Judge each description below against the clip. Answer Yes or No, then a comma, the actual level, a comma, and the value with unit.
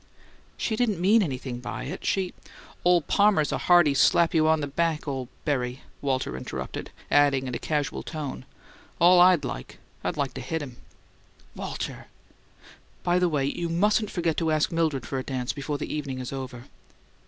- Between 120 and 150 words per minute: No, average, 180 wpm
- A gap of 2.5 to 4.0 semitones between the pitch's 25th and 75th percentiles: No, average, 4.6 semitones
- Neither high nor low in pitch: Yes, medium, 150 Hz